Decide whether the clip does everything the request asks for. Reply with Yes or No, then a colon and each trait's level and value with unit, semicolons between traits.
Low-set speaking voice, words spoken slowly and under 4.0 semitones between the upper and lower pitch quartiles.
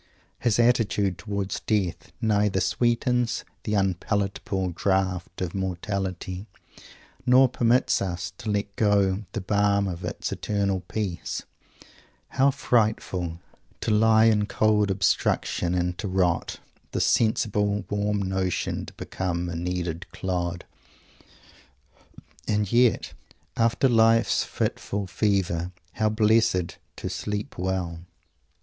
Yes: low, 100 Hz; slow, 110 wpm; average, 2.9 semitones